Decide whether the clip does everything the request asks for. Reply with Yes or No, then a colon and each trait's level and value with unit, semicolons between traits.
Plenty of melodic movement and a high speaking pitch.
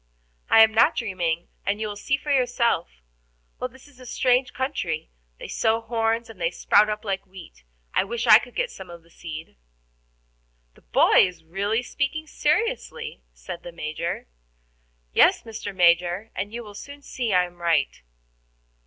Yes: wide, 5.8 semitones; high, 210 Hz